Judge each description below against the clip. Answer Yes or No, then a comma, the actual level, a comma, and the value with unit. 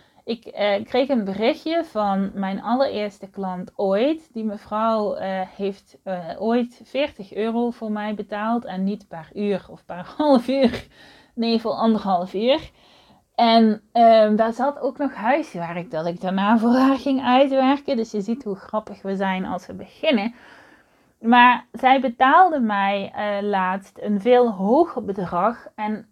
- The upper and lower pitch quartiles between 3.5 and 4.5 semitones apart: Yes, average, 4.0 semitones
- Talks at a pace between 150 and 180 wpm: Yes, average, 155 wpm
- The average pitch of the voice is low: No, high, 220 Hz